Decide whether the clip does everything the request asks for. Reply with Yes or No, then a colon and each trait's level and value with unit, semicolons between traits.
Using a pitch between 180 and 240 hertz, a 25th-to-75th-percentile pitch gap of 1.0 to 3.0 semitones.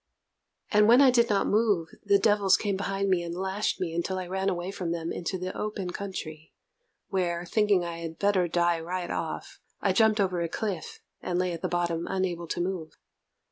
Yes: medium, 185 Hz; narrow, 2.6 semitones